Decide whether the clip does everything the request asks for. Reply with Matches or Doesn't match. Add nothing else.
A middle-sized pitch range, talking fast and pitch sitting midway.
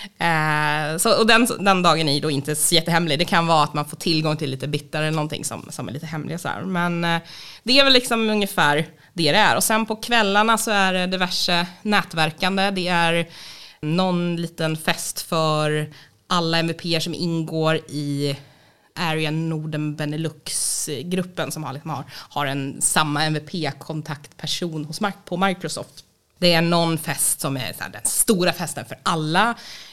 Doesn't match